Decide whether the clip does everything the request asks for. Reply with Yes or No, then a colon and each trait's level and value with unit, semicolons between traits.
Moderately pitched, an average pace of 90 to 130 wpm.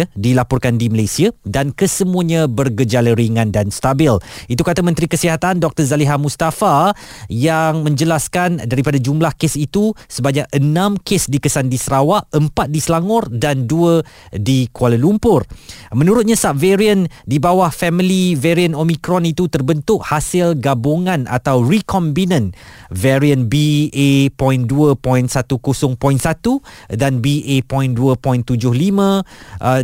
Yes: medium, 145 Hz; average, 110 wpm